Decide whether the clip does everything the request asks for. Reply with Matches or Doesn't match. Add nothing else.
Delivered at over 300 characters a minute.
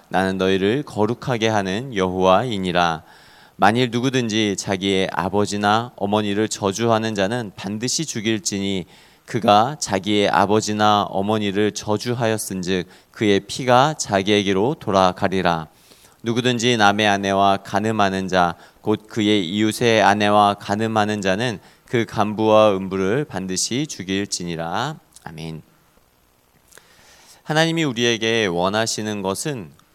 Doesn't match